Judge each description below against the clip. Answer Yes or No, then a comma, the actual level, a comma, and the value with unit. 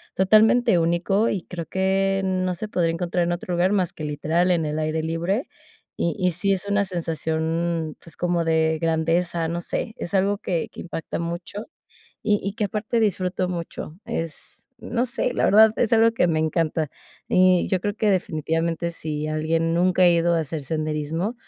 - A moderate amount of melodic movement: Yes, average, 3.0 semitones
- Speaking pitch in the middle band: Yes, medium, 175 Hz